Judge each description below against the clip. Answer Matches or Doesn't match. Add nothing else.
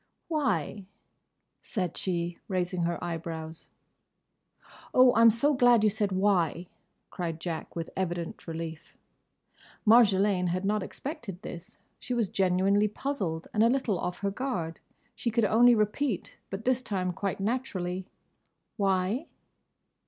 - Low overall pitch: Doesn't match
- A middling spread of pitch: Matches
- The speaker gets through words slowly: Matches